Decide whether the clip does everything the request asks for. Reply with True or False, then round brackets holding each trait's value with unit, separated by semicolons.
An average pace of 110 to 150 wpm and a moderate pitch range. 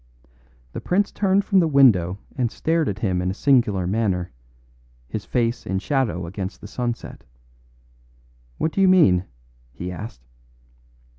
False (145 wpm; 7.6 semitones)